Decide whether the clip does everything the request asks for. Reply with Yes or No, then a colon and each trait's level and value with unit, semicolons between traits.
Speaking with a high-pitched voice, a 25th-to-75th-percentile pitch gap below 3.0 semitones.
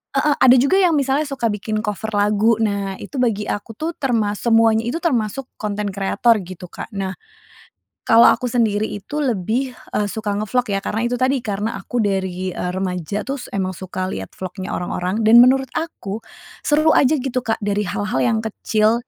No: high, 220 Hz; average, 3.8 semitones